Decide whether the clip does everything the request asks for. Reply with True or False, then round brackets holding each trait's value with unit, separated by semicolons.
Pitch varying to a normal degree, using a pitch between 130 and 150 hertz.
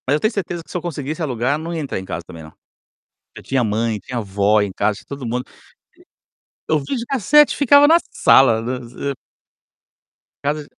False (7.7 semitones; 140 Hz)